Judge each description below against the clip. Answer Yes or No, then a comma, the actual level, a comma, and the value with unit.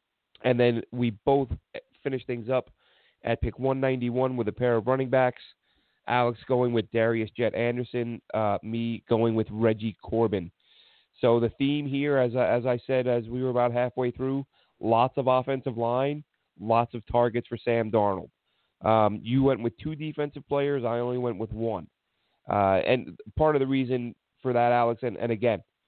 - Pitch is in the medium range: No, low, 120 Hz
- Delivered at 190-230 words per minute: No, average, 175 wpm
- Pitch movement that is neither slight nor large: No, narrow, 2.2 semitones